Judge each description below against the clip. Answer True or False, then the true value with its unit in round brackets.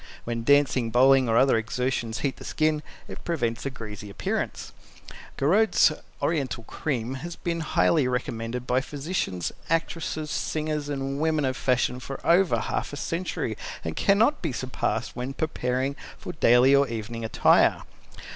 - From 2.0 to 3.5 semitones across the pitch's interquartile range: False (4.5 semitones)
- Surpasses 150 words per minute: False (145 wpm)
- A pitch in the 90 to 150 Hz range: True (135 Hz)